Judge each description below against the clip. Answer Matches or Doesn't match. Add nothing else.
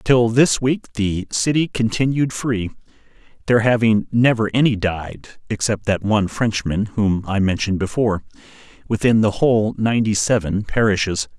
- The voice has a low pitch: Matches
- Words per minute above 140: Doesn't match